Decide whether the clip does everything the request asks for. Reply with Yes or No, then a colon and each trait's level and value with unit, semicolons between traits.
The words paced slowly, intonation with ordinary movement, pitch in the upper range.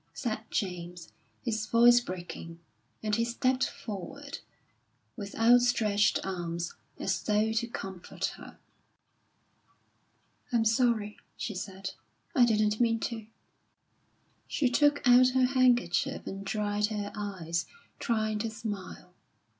Yes: slow, 115 wpm; average, 3.5 semitones; high, 215 Hz